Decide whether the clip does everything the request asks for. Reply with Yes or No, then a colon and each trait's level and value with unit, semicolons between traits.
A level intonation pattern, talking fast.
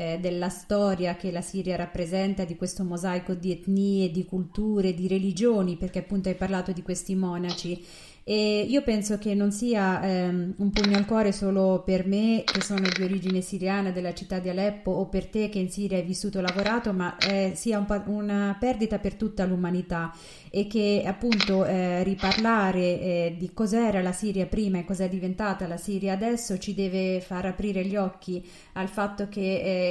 Yes: narrow, 1.8 semitones; fast, 185 wpm